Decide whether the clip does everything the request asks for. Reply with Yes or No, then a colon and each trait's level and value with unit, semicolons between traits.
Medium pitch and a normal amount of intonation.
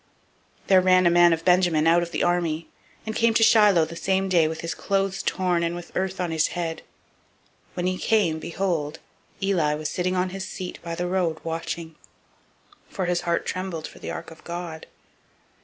No: medium, 175 Hz; narrow, 2.2 semitones